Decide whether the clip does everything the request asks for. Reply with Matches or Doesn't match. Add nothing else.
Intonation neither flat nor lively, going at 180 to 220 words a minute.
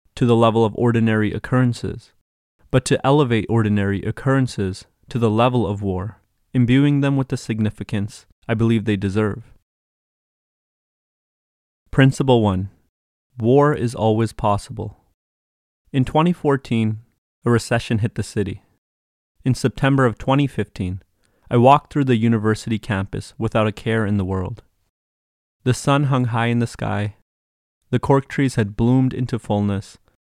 Doesn't match